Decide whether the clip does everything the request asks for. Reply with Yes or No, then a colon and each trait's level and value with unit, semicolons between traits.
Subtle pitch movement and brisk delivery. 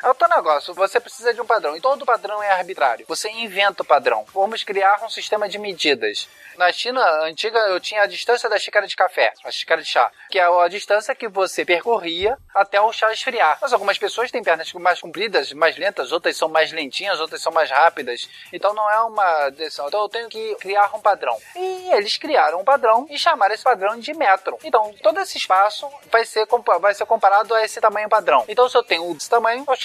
No: average, 4.0 semitones; fast, 215 wpm